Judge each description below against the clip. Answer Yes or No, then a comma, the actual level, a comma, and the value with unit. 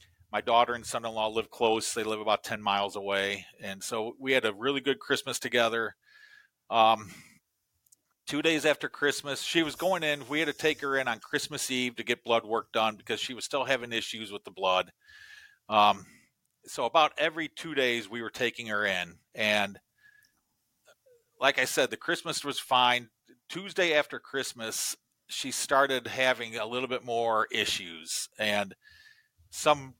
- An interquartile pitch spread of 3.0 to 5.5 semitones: Yes, average, 5.1 semitones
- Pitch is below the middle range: Yes, low, 125 Hz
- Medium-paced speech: Yes, average, 175 wpm